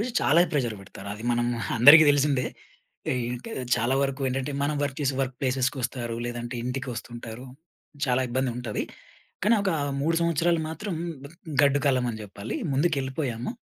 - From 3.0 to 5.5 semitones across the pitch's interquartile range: Yes, average, 3.3 semitones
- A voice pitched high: No, low, 130 Hz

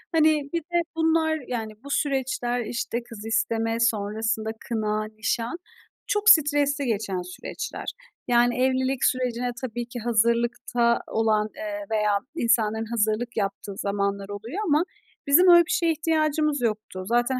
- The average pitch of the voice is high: Yes, high, 240 Hz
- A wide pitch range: No, average, 4.9 semitones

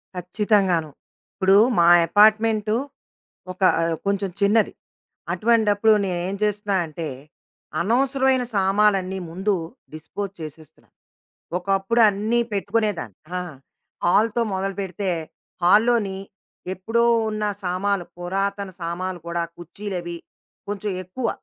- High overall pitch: Yes, high, 200 Hz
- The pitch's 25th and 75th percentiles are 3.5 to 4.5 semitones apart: No, average, 2.8 semitones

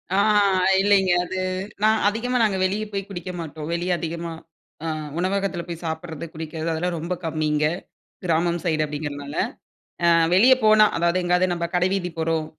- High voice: No, medium, 175 Hz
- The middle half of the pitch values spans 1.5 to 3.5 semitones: Yes, average, 3.1 semitones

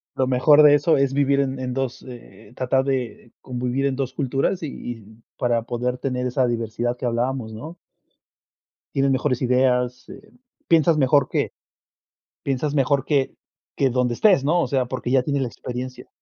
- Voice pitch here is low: Yes, low, 130 Hz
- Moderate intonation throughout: No, narrow, 2.0 semitones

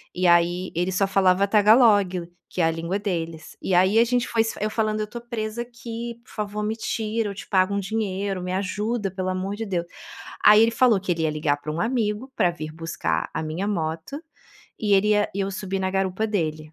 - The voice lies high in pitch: Yes, high, 195 Hz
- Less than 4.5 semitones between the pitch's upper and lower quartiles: Yes, average, 3.4 semitones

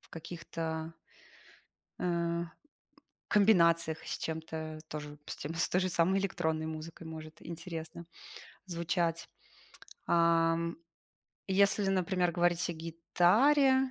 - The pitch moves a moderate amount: No, narrow, 2.0 semitones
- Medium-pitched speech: Yes, medium, 170 Hz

